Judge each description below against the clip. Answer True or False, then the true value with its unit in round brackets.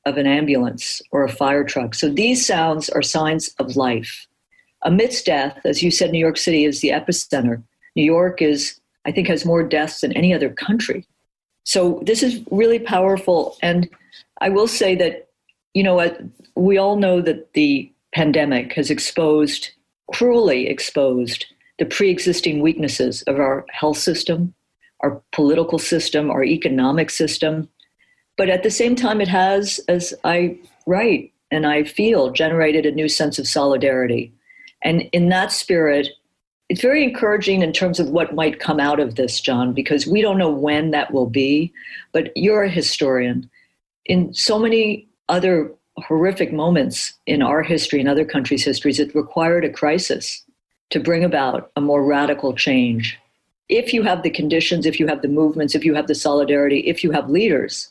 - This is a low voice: False (160 Hz)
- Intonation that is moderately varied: True (3.8 semitones)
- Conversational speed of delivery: True (170 wpm)